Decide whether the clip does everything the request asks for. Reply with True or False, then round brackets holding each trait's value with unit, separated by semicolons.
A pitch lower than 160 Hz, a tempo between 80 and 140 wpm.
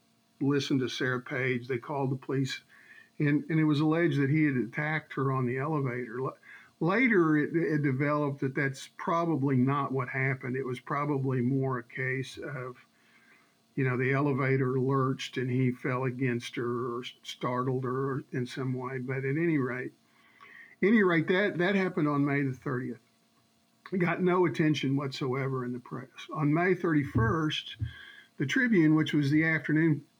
False (135 Hz; 165 wpm)